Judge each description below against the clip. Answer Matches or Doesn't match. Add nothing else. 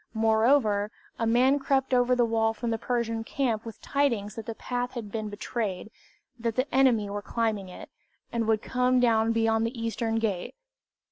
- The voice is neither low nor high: Doesn't match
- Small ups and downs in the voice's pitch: Matches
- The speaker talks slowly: Doesn't match